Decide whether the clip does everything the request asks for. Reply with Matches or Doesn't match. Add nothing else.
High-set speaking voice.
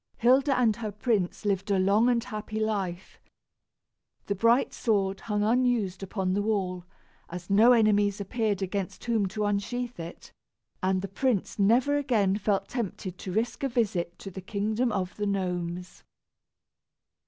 Matches